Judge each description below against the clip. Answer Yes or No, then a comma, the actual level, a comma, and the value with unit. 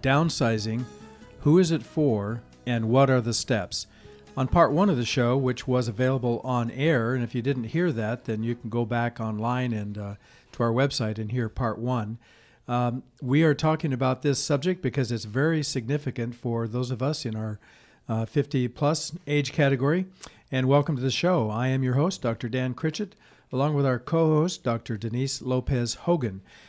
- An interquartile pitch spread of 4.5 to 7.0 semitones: No, average, 3.6 semitones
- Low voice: Yes, low, 130 Hz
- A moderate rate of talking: Yes, average, 190 wpm